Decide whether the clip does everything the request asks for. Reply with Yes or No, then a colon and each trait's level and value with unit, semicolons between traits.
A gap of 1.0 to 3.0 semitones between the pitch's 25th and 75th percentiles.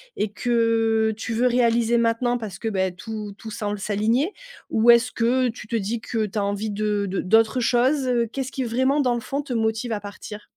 Yes: narrow, 2.4 semitones